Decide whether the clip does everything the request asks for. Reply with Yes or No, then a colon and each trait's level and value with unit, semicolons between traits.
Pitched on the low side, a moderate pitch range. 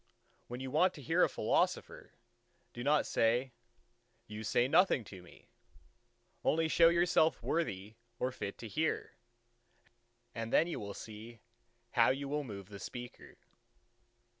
No: low, 125 Hz; wide, 6.2 semitones